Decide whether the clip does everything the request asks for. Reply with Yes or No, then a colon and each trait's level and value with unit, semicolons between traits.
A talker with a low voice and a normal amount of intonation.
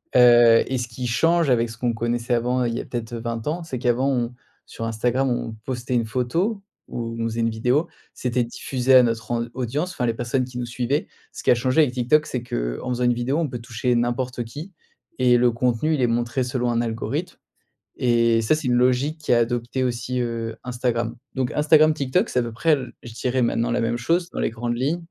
No: low, 120 Hz; narrow, 1.8 semitones